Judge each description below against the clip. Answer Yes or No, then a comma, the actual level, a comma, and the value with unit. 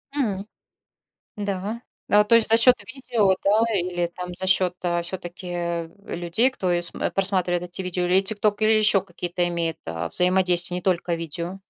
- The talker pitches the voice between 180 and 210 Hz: Yes, medium, 185 Hz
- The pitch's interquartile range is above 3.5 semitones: No, average, 2.7 semitones